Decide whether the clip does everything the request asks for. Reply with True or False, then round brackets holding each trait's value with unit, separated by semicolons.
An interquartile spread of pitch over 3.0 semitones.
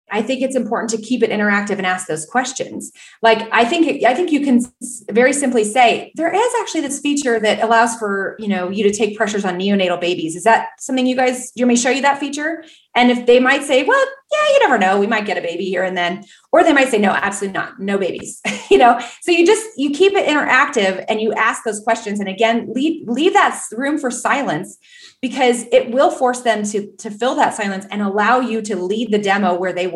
True (4.7 semitones)